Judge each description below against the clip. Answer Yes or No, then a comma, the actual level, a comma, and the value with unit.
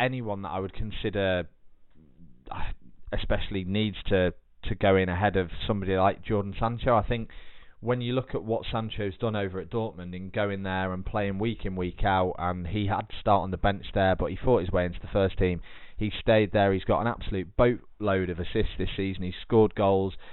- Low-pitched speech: Yes, low, 100 Hz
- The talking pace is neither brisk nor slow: No, fast, 210 wpm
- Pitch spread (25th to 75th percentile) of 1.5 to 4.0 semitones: Yes, average, 2.7 semitones